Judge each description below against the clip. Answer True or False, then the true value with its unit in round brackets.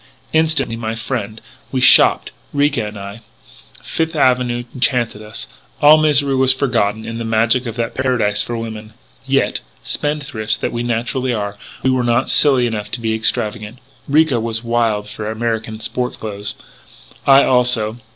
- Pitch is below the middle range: True (120 Hz)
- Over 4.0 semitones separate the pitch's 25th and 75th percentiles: False (3.0 semitones)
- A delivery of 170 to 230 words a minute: False (155 wpm)